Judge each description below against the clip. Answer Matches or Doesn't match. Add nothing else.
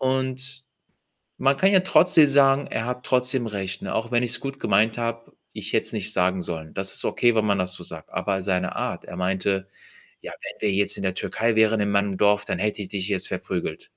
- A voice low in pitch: Matches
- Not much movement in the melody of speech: Doesn't match